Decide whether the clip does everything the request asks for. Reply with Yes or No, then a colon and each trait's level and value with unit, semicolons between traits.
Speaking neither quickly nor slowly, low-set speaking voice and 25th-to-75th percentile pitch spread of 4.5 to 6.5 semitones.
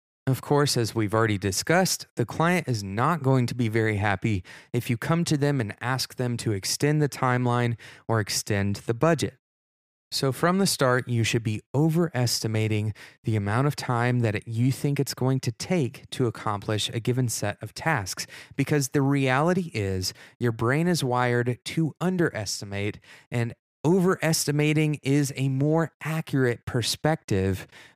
Yes: average, 160 wpm; low, 125 Hz; average, 4.8 semitones